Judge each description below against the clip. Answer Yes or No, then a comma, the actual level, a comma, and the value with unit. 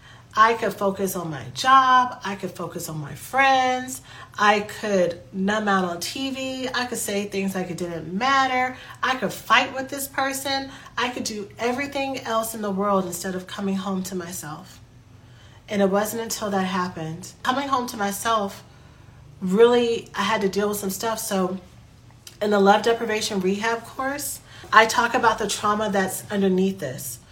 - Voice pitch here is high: Yes, high, 205 Hz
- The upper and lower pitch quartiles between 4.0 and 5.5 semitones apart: Yes, average, 4.4 semitones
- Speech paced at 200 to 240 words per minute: No, average, 175 wpm